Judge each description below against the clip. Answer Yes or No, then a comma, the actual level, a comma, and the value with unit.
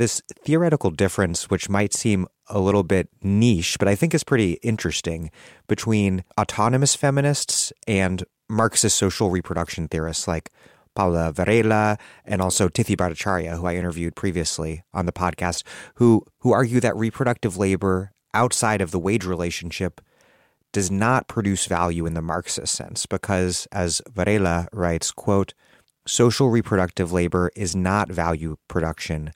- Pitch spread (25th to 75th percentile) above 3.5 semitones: Yes, average, 4.2 semitones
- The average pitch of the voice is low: Yes, very low, 95 Hz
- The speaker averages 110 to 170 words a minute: Yes, average, 140 wpm